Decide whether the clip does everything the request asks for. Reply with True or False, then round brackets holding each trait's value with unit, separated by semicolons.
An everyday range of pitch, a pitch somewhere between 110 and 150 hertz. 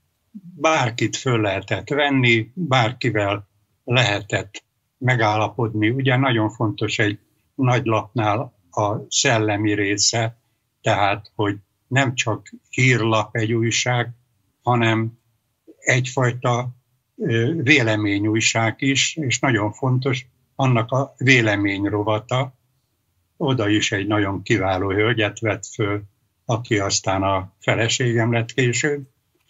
True (3.2 semitones; 115 Hz)